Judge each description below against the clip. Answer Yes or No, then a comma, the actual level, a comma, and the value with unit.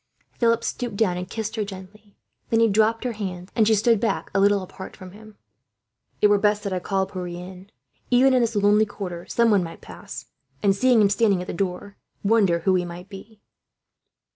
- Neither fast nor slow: No, fast, 215 wpm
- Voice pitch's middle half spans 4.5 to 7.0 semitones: No, average, 3.0 semitones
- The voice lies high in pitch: Yes, high, 205 Hz